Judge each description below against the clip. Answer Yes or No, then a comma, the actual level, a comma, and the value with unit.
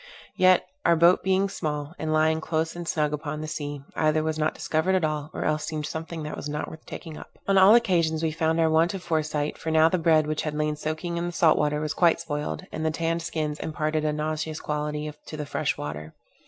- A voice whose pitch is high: No, medium, 155 Hz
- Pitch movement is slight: Yes, narrow, 1.5 semitones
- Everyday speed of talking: No, fast, 235 wpm